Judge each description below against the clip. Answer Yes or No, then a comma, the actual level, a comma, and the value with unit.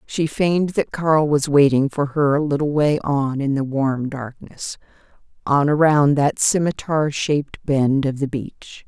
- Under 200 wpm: Yes, average, 160 wpm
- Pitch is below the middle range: No, medium, 145 Hz